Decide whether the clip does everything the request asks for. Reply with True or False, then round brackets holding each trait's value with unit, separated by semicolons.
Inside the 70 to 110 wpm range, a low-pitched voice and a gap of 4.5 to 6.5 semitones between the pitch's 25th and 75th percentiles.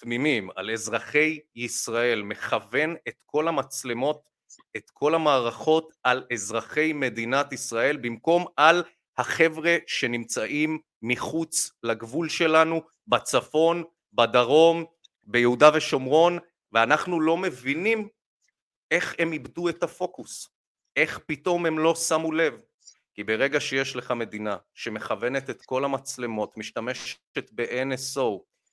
False (105 wpm; 145 Hz; 5.3 semitones)